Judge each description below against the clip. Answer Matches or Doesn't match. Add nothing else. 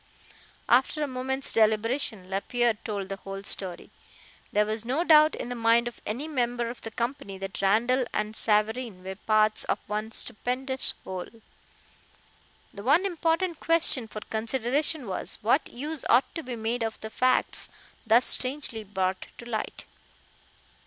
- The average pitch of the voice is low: Doesn't match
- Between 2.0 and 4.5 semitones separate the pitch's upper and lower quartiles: Matches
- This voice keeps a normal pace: Matches